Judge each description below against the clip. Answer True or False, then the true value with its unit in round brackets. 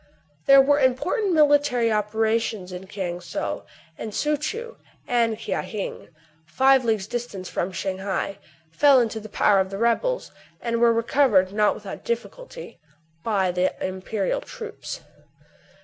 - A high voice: True (230 Hz)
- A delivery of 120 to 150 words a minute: True (140 wpm)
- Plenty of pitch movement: True (6.4 semitones)